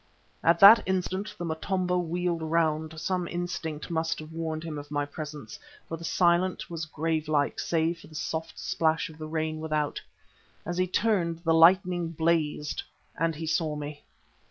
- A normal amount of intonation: No, narrow, 2.0 semitones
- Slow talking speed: No, average, 165 wpm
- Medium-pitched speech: Yes, medium, 165 Hz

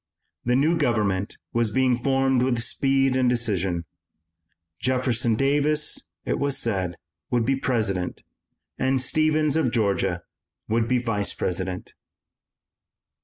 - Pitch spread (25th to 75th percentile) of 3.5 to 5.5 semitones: Yes, average, 4.1 semitones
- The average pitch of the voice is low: Yes, low, 125 Hz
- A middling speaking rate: No, slow, 120 wpm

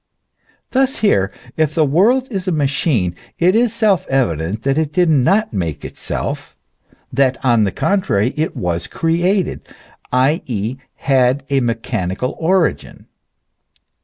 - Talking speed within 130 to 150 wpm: Yes, slow, 135 wpm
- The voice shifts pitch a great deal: Yes, wide, 7.7 semitones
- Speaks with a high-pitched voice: No, medium, 140 Hz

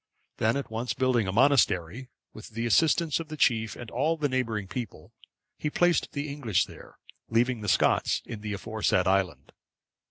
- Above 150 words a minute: Yes, average, 170 wpm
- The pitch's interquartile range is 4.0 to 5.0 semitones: Yes, average, 4.7 semitones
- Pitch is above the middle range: No, low, 120 Hz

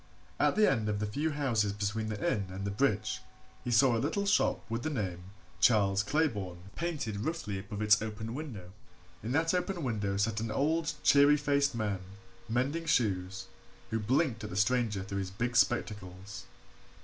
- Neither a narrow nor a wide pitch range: No, wide, 5.7 semitones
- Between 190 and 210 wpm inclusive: No, average, 175 wpm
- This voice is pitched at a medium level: No, low, 110 Hz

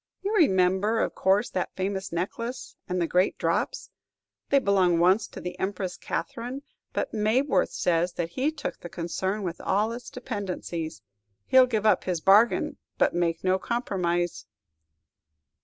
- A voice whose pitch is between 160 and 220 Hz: Yes, high, 190 Hz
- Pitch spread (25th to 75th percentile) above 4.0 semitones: Yes, average, 4.6 semitones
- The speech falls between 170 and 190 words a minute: No, average, 155 wpm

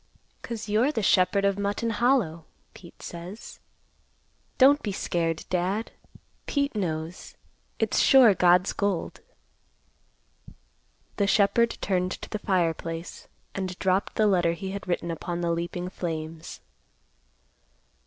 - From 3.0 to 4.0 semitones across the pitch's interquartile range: Yes, average, 3.5 semitones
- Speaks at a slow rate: Yes, slow, 120 wpm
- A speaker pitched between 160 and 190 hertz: Yes, medium, 185 Hz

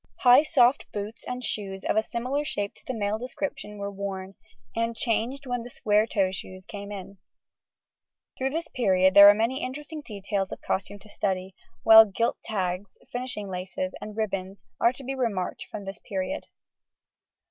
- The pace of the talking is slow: No, average, 170 wpm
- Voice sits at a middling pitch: No, high, 210 Hz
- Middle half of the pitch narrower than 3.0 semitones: No, average, 4.1 semitones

